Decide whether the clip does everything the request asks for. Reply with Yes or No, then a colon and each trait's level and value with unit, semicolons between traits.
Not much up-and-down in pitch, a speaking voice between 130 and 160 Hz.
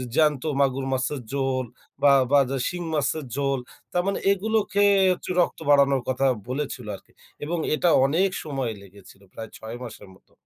No: average, 3.7 semitones; medium, 140 Hz